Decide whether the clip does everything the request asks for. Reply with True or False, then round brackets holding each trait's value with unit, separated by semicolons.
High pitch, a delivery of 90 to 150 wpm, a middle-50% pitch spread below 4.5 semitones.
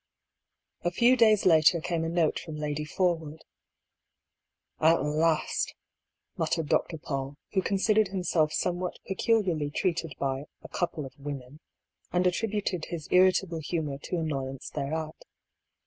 False (165 Hz; 145 wpm; 3.4 semitones)